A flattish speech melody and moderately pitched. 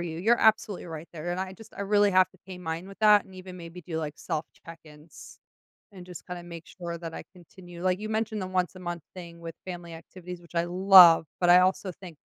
Yes: narrow, 1.9 semitones; medium, 180 Hz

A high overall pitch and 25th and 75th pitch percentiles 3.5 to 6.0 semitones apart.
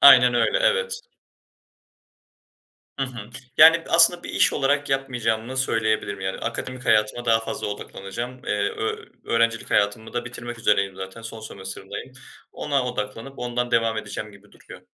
No: low, 120 Hz; average, 4.0 semitones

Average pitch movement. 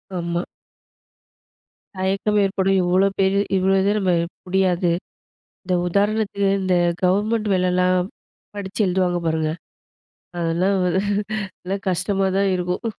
No: narrow, 1.6 semitones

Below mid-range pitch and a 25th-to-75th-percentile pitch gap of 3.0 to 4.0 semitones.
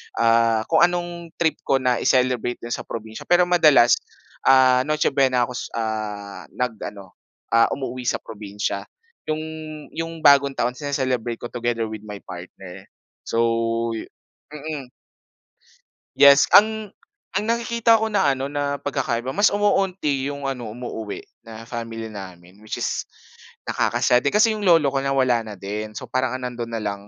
No: low, 125 Hz; average, 4.8 semitones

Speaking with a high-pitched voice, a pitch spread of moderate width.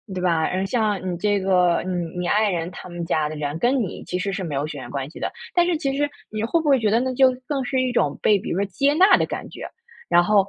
No: high, 195 Hz; wide, 6.3 semitones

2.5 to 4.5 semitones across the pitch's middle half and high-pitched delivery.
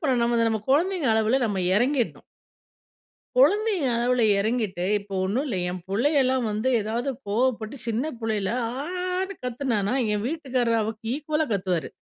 No: average, 5.1 semitones; high, 245 Hz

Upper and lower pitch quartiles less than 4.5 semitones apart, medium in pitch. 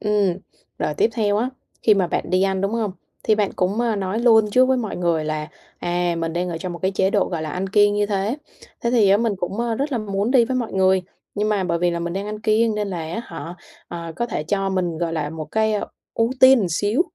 No: average, 3.7 semitones; high, 195 Hz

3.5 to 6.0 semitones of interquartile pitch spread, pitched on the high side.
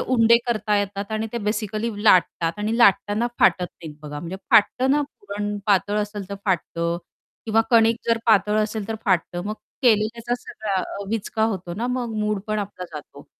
No: narrow, 2.6 semitones; high, 210 Hz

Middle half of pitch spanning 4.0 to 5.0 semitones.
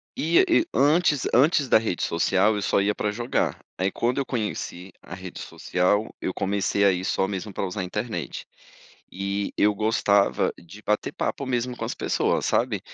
Yes: average, 4.3 semitones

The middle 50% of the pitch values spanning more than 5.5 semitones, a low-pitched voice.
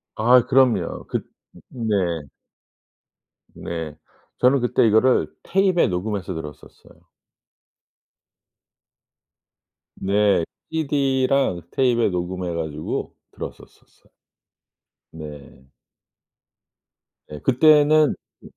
Yes: wide, 7.4 semitones; low, 110 Hz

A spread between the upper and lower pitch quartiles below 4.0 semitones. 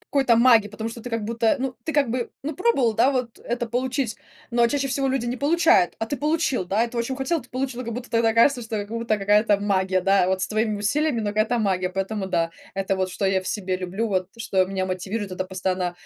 No: average, 4.5 semitones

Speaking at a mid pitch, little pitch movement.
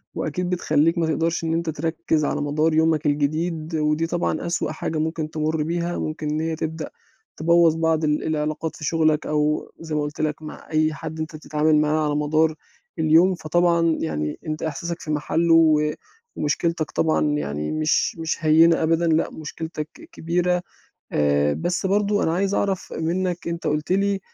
Yes: medium, 160 Hz; narrow, 1.7 semitones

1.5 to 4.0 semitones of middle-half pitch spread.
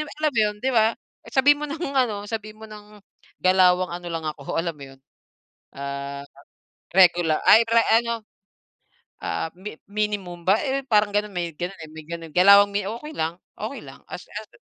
No: average, 4.6 semitones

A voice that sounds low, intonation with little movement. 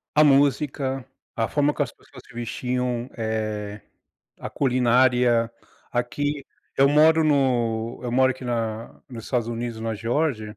No: low, 125 Hz; average, 3.1 semitones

